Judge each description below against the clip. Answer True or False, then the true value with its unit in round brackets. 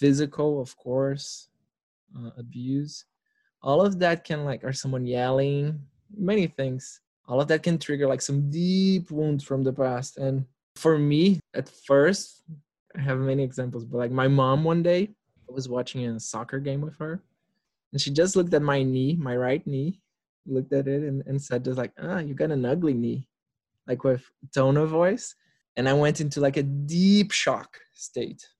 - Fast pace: False (185 wpm)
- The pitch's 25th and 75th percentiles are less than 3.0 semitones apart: False (3.4 semitones)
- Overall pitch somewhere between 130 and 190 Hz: True (140 Hz)